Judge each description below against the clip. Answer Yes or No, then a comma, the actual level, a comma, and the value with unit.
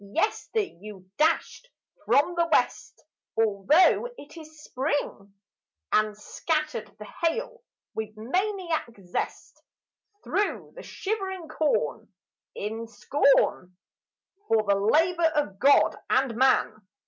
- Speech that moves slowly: Yes, slow, 105 wpm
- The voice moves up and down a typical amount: No, wide, 8.0 semitones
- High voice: Yes, very high, 285 Hz